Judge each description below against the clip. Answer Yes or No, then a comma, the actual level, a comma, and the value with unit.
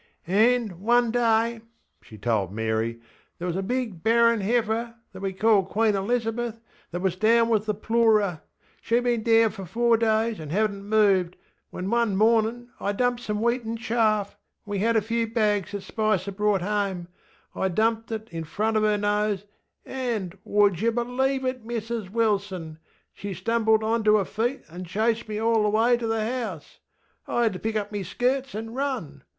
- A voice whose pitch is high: Yes, high, 220 Hz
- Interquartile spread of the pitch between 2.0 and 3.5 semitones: Yes, average, 2.8 semitones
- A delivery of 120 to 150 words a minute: No, average, 175 wpm